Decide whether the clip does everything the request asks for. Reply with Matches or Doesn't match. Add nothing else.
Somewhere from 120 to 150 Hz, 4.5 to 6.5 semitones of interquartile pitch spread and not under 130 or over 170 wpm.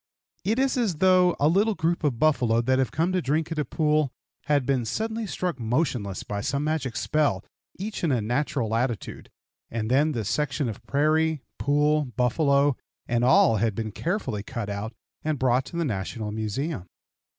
Doesn't match